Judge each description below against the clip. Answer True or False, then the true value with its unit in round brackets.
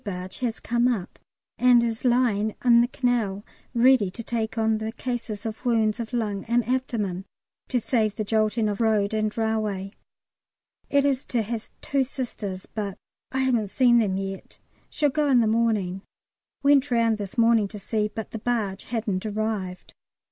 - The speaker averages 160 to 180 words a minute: True (170 wpm)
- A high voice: True (225 Hz)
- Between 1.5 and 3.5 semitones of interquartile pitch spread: True (2.7 semitones)